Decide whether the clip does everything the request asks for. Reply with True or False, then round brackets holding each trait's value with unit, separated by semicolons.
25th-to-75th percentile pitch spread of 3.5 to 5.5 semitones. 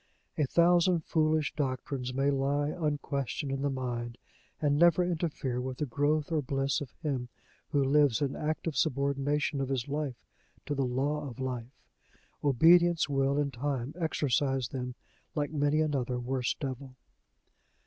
False (2.4 semitones)